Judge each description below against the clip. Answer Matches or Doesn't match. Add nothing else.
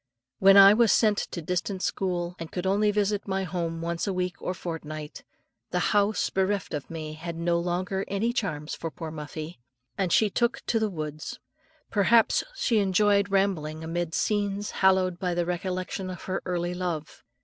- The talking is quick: Doesn't match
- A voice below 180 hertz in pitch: Doesn't match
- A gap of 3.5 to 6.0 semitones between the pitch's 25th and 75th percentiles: Doesn't match